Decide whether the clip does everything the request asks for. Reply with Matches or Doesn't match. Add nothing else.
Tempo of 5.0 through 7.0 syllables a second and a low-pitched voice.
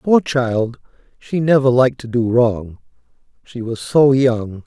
Doesn't match